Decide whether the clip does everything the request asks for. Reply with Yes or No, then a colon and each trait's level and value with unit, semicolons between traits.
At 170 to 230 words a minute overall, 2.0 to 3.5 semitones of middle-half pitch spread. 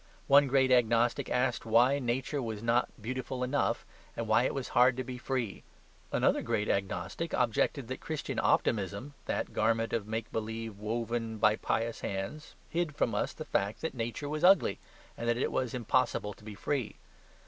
Yes: average, 175 wpm; average, 2.9 semitones